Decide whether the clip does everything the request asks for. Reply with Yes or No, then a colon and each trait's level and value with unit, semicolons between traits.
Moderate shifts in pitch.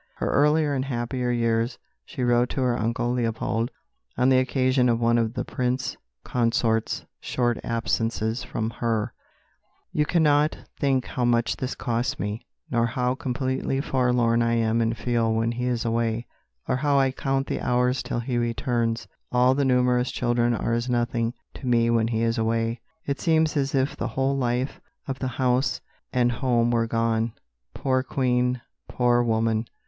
No: narrow, 1.9 semitones